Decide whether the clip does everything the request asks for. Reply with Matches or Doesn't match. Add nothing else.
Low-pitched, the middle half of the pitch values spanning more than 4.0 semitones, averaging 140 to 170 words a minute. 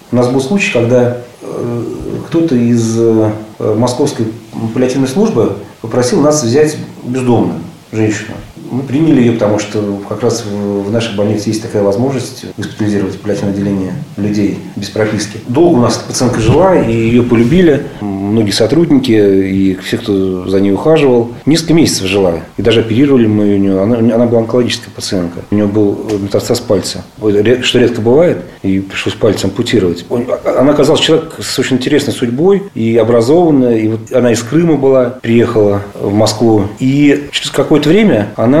Doesn't match